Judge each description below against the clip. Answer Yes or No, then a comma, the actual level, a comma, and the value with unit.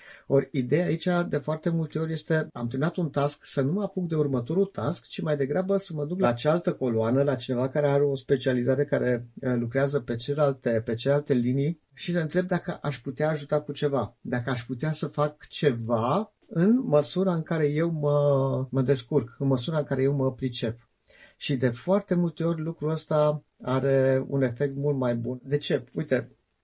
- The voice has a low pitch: No, medium, 145 Hz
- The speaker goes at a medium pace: No, fast, 195 wpm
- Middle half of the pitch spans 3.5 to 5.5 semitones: No, average, 3.1 semitones